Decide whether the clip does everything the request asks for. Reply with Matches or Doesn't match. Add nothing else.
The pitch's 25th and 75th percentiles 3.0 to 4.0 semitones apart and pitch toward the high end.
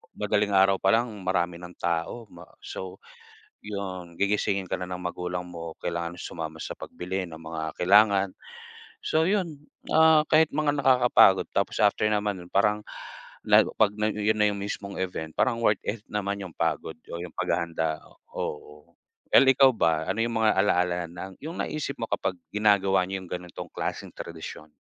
Doesn't match